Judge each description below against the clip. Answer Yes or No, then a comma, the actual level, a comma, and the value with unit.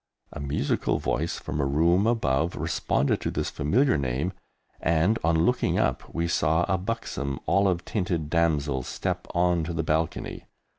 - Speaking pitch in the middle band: No, very low, 80 Hz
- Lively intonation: No, average, 3.1 semitones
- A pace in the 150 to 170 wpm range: Yes, average, 155 wpm